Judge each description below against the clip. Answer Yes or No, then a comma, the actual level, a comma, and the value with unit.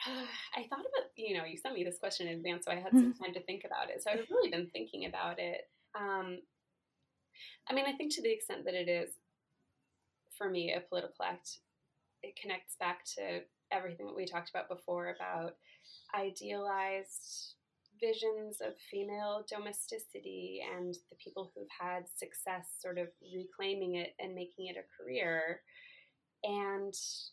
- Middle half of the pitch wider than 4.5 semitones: No, average, 3.1 semitones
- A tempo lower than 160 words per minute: No, average, 165 wpm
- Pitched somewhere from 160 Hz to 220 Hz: Yes, medium, 185 Hz